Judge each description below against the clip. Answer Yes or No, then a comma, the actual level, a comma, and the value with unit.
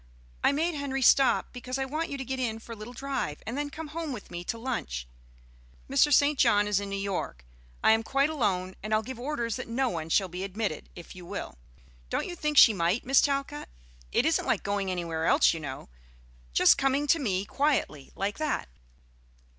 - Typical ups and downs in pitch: No, wide, 6.7 semitones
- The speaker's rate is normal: No, fast, 210 wpm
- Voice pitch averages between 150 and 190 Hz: No, high, 230 Hz